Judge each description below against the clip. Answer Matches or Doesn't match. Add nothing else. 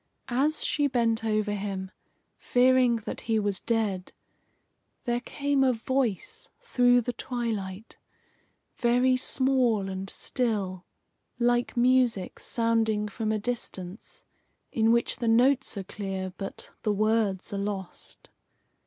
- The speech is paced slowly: Matches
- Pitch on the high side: Matches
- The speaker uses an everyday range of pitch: Matches